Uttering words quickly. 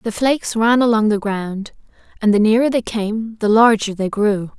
No: average, 195 wpm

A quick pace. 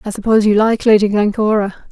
No: average, 190 wpm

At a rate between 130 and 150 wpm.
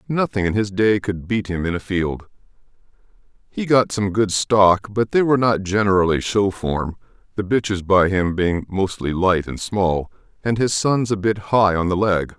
No: average, 195 wpm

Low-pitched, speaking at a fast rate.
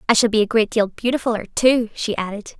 No: high, 225 Hz; fast, 230 wpm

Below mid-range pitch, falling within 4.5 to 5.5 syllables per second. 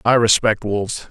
Yes: low, 110 Hz; 5.0 syllables/s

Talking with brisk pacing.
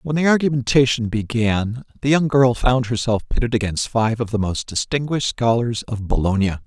No: average, 170 wpm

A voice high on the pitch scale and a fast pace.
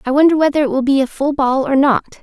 Yes: very high, 270 Hz; fast, 295 wpm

